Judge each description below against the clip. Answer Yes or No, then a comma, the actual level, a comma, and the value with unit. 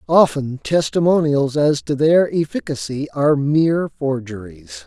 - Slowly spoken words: Yes, slow, 110 wpm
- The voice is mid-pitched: Yes, medium, 145 Hz